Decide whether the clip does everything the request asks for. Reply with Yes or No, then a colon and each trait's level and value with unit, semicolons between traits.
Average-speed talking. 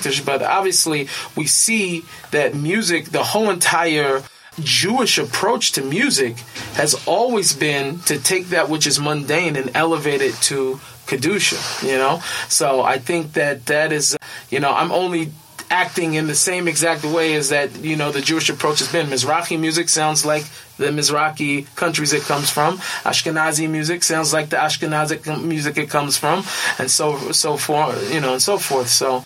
Yes: average, 170 wpm